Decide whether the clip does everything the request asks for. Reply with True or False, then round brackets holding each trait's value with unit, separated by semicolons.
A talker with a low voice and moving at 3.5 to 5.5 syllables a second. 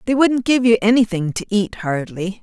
False (215 Hz; 5.1 syllables/s)